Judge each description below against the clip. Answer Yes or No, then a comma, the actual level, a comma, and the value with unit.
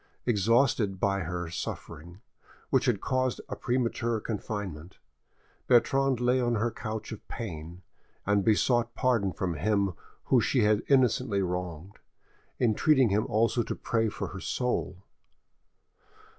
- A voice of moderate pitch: No, low, 110 Hz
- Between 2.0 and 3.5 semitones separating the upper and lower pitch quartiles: No, average, 4.1 semitones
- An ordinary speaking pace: No, slow, 130 wpm